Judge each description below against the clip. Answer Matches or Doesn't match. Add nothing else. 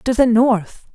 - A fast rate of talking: Doesn't match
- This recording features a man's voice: Doesn't match